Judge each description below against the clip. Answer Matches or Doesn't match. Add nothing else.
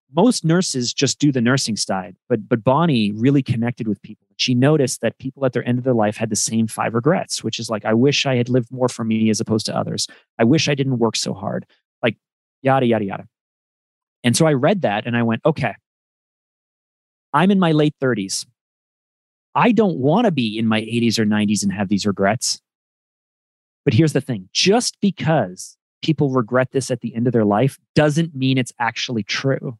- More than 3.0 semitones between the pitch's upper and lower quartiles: Matches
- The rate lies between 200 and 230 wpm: Matches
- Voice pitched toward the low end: Matches